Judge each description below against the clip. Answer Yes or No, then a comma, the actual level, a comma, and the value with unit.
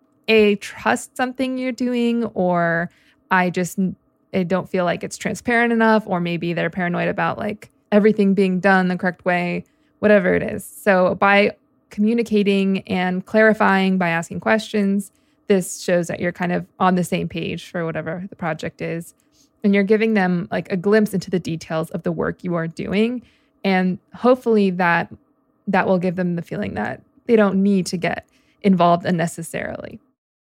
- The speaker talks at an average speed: Yes, average, 170 wpm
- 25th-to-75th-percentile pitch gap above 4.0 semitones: No, average, 3.4 semitones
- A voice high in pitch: Yes, high, 195 Hz